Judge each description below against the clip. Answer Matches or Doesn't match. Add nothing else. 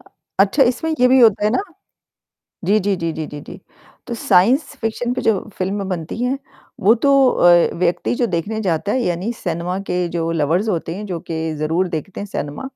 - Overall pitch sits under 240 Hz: Matches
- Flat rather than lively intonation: Doesn't match